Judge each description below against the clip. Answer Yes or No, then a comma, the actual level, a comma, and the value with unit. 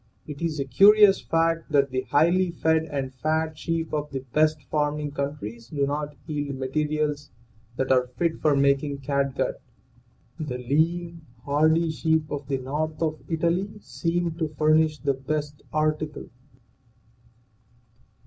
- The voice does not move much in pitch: Yes, narrow, 2.3 semitones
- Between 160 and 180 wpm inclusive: No, average, 140 wpm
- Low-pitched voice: No, medium, 150 Hz